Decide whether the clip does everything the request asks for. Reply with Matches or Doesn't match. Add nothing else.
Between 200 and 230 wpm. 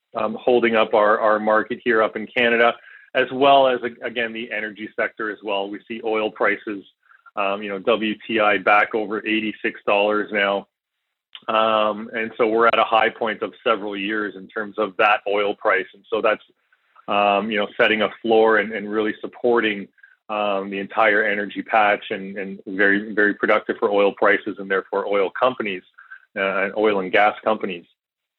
Doesn't match